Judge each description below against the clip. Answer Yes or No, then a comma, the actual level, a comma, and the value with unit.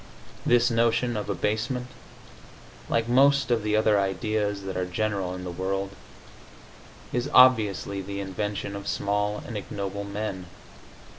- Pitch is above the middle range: No, low, 105 Hz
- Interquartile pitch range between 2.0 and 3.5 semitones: Yes, average, 2.7 semitones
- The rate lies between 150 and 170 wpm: No, slow, 135 wpm